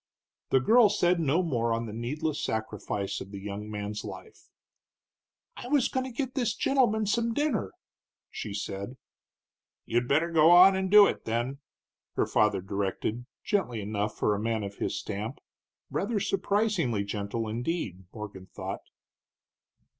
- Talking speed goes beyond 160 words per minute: No, average, 150 wpm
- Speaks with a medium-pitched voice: No, low, 120 Hz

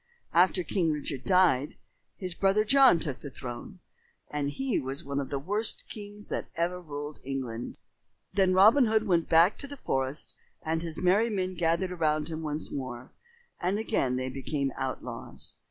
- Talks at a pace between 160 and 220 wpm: Yes, average, 170 wpm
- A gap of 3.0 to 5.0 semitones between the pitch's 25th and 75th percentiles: No, wide, 5.6 semitones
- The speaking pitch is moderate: Yes, medium, 165 Hz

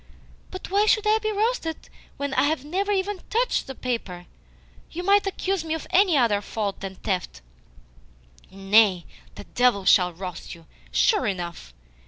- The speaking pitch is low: No, very high, 270 Hz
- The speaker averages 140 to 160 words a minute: Yes, average, 155 wpm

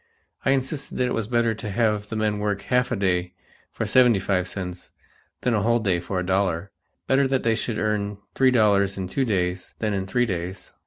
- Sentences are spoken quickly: Yes, fast, 215 wpm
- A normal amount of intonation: Yes, average, 3.8 semitones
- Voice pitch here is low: Yes, low, 105 Hz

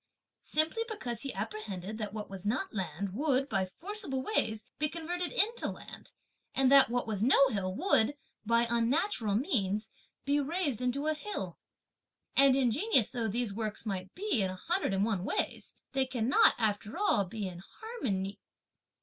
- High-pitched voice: Yes, high, 235 Hz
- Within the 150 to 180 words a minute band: Yes, average, 165 wpm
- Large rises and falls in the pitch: Yes, wide, 6.3 semitones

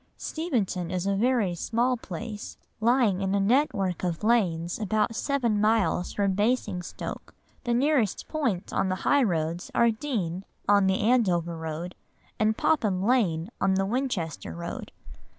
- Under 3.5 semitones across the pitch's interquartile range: No, average, 4.8 semitones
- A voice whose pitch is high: Yes, high, 205 Hz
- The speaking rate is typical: Yes, average, 145 wpm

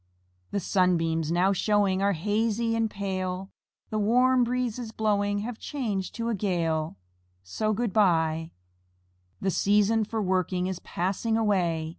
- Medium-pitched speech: No, high, 200 Hz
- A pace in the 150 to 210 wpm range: No, slow, 135 wpm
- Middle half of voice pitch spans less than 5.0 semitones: Yes, average, 3.3 semitones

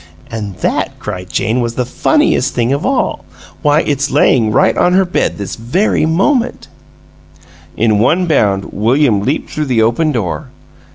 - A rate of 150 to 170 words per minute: Yes, average, 160 wpm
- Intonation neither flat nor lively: No, wide, 6.3 semitones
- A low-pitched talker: Yes, low, 130 Hz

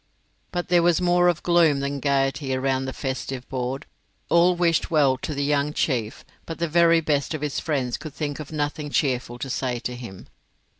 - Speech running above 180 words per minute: Yes, average, 200 wpm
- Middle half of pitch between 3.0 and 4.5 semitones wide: Yes, average, 3.7 semitones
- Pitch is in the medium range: Yes, medium, 145 Hz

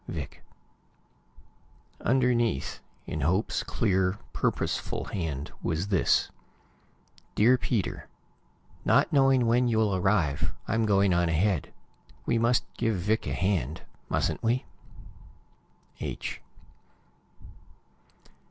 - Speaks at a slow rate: Yes, slow, 95 wpm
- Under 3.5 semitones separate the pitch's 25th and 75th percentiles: No, average, 4.8 semitones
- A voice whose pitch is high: No, low, 100 Hz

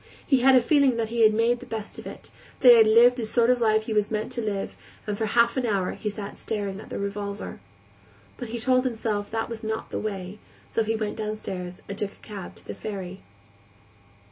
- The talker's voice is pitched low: No, high, 220 Hz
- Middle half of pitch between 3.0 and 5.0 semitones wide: No, narrow, 2.4 semitones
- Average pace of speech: No, fast, 235 wpm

